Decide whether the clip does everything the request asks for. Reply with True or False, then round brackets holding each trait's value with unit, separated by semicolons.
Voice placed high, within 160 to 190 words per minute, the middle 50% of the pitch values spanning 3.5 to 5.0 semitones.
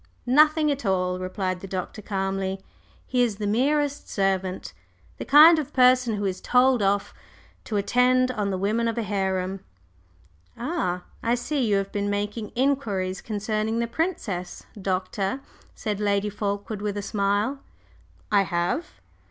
False (205 Hz; 150 wpm; 4.3 semitones)